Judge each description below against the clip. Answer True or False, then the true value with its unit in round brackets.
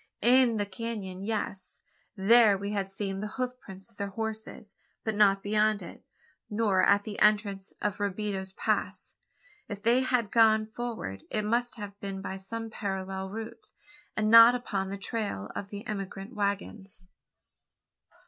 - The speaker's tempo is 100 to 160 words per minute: True (155 wpm)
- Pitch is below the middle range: False (205 Hz)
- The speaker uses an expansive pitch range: False (2.4 semitones)